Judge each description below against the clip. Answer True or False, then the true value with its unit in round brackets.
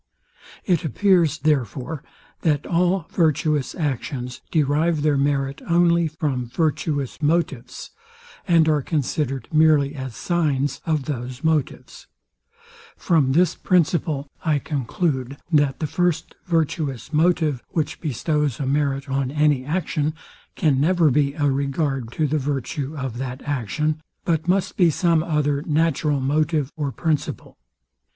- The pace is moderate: False (130 wpm)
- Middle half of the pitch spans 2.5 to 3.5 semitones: True (2.9 semitones)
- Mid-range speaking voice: True (150 Hz)